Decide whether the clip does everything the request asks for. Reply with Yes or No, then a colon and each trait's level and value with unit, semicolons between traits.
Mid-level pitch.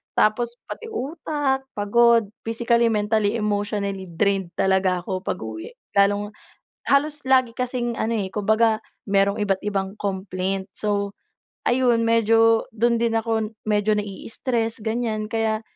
No: high, 215 Hz